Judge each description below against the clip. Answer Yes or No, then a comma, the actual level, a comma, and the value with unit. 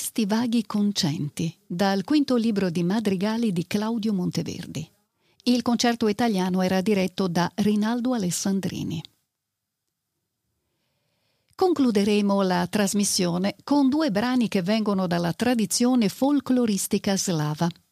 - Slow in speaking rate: Yes, slow, 105 wpm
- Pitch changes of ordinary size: Yes, average, 4.1 semitones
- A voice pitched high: Yes, high, 205 Hz